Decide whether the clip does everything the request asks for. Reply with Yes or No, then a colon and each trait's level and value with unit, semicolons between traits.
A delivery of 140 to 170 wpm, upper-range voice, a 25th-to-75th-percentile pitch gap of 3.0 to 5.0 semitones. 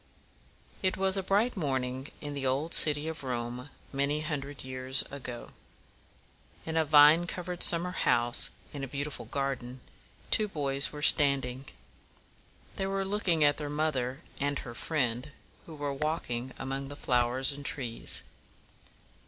No: average, 145 wpm; medium, 140 Hz; average, 3.3 semitones